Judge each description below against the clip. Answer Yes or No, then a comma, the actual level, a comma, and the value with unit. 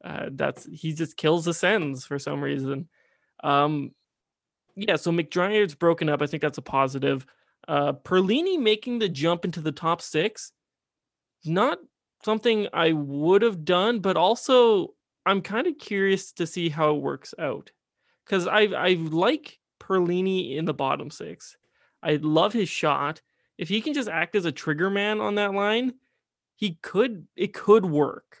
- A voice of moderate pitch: Yes, medium, 180 Hz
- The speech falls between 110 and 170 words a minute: Yes, average, 165 wpm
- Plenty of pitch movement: No, average, 5.0 semitones